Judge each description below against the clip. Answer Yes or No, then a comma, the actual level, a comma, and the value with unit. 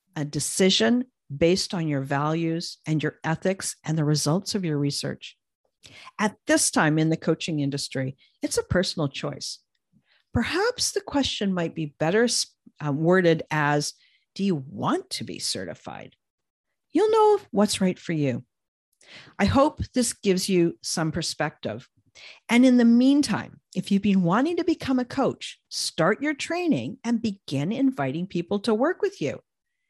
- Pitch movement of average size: No, wide, 8.0 semitones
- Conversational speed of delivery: Yes, average, 155 wpm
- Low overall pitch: No, high, 190 Hz